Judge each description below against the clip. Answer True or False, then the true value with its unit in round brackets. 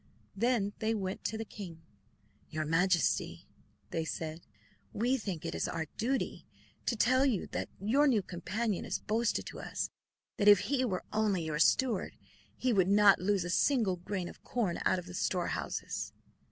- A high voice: True (200 Hz)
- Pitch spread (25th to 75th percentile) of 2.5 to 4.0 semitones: False (4.6 semitones)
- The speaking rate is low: False (165 wpm)